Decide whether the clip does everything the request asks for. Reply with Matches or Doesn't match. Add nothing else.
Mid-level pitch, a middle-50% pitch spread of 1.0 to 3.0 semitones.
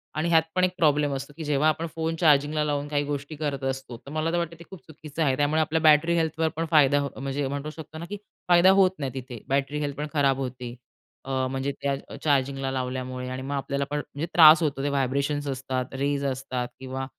Matches